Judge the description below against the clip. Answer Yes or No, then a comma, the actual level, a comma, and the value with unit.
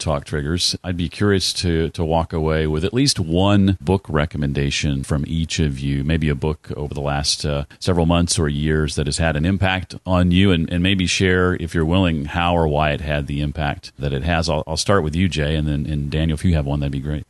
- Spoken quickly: Yes, fast, 245 wpm